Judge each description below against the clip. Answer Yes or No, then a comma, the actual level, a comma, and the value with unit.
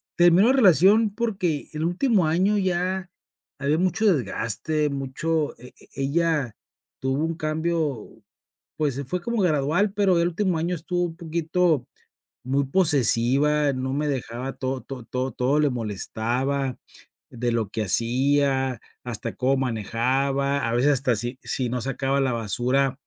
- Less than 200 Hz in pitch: Yes, medium, 140 Hz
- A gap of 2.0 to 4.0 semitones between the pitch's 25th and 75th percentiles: No, average, 5.0 semitones